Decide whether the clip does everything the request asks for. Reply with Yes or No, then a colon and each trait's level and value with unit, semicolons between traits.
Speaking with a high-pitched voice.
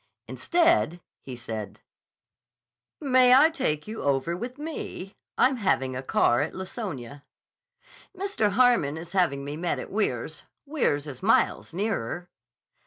No: medium, 180 Hz